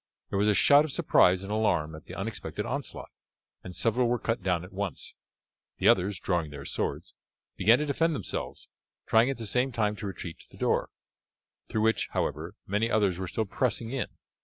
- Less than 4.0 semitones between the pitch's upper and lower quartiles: No, average, 4.6 semitones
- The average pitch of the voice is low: Yes, low, 105 Hz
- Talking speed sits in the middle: Yes, average, 195 wpm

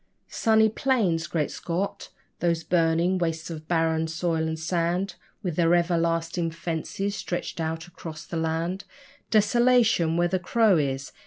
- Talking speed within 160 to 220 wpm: No, average, 140 wpm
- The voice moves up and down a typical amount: No, narrow, 2.3 semitones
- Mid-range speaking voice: Yes, medium, 170 Hz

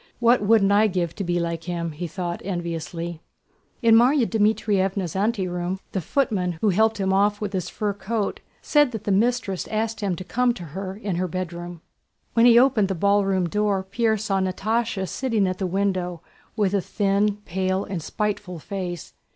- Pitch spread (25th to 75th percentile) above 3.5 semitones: No, average, 3.2 semitones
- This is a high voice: Yes, high, 195 Hz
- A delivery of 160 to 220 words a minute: Yes, average, 175 wpm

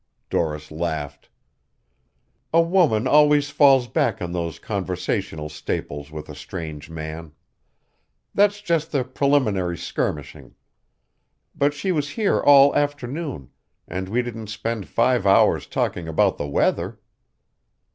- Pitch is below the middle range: Yes, low, 110 Hz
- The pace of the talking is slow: Yes, slow, 120 wpm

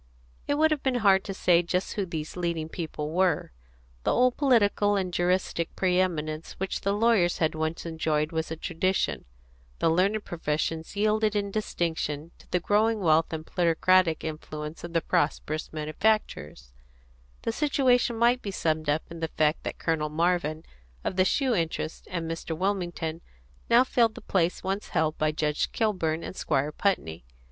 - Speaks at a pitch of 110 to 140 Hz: No, medium, 175 Hz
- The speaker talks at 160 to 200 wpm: Yes, average, 170 wpm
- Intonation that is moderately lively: Yes, average, 4.3 semitones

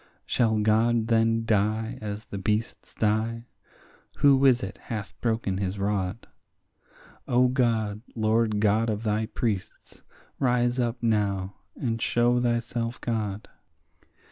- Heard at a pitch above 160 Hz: No, low, 110 Hz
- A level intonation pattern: Yes, narrow, 2.0 semitones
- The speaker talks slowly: Yes, slow, 120 wpm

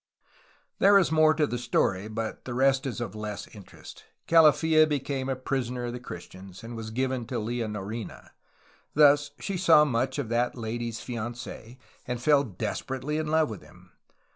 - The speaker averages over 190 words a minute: No, average, 165 wpm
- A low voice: Yes, low, 125 Hz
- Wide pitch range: No, average, 4.4 semitones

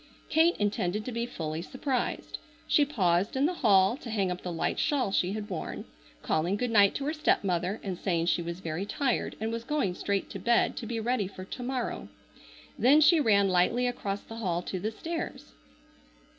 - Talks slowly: No, average, 200 wpm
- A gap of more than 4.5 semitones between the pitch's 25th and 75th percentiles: Yes, average, 5.2 semitones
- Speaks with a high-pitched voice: Yes, high, 210 Hz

